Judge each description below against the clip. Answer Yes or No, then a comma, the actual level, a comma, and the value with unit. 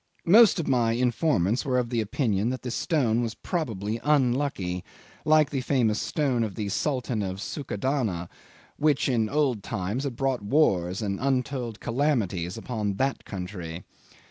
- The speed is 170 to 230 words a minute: No, average, 155 wpm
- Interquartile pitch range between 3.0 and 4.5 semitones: No, average, 5.2 semitones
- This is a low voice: Yes, low, 120 Hz